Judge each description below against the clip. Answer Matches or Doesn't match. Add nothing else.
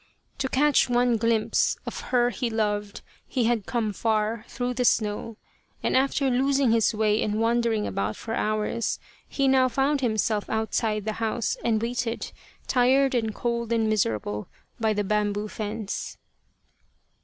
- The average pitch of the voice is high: Matches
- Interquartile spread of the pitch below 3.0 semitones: Matches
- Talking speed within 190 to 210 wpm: Doesn't match